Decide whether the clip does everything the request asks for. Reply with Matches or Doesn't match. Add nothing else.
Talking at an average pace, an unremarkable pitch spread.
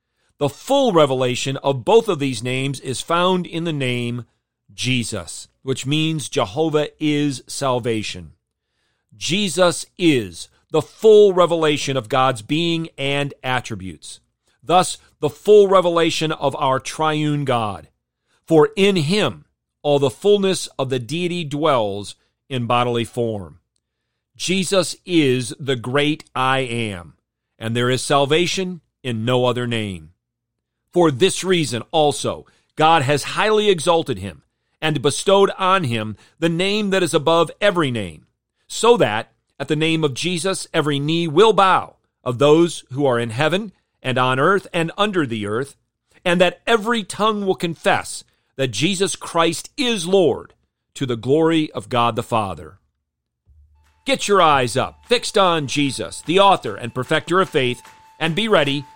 Doesn't match